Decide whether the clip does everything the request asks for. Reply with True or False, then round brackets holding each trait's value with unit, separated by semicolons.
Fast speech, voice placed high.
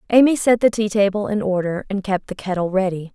True (230 wpm; 200 Hz)